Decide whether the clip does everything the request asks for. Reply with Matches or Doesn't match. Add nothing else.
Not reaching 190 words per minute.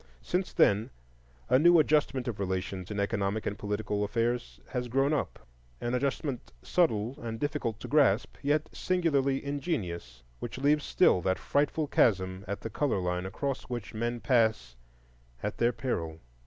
Matches